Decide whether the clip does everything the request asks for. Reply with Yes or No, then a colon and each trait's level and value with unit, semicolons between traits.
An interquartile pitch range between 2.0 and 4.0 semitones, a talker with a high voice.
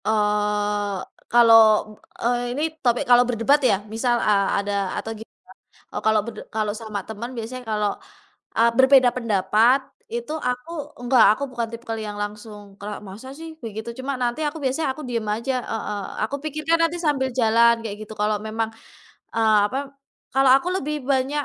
Yes: average, 3.5 semitones; high, 230 Hz